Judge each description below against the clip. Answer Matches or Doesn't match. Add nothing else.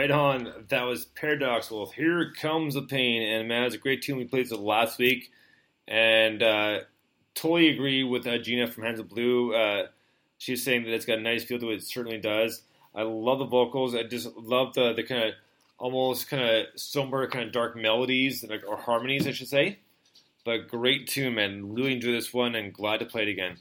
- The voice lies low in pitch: Matches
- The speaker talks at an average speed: Doesn't match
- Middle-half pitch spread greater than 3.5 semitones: Doesn't match